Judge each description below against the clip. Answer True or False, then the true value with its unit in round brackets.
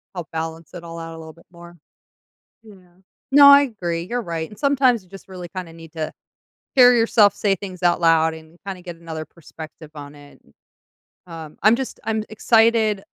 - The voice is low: False (175 Hz)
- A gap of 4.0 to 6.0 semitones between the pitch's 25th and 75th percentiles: True (5.0 semitones)